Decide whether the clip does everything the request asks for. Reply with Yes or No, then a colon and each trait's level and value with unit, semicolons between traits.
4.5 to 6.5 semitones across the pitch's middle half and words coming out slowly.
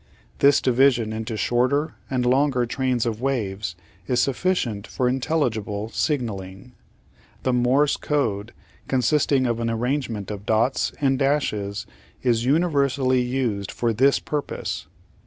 No: average, 3.7 semitones; slow, 125 wpm